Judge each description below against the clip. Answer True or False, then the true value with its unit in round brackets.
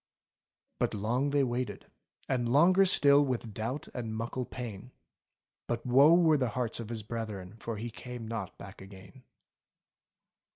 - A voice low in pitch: True (120 Hz)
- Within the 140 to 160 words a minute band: True (150 wpm)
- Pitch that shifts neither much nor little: True (3.2 semitones)